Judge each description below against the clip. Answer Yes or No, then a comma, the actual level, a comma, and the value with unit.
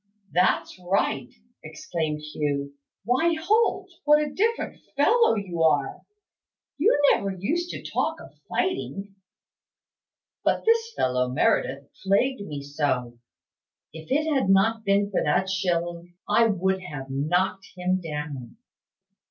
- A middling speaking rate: No, slow, 125 wpm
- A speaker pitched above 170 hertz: Yes, medium, 185 Hz